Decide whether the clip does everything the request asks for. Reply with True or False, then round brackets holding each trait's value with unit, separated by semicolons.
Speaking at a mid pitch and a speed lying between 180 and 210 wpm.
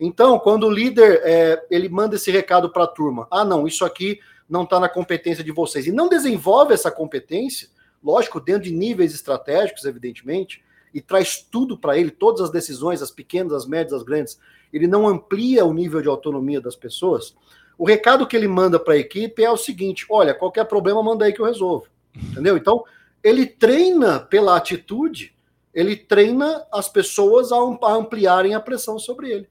False (200 Hz; 185 wpm)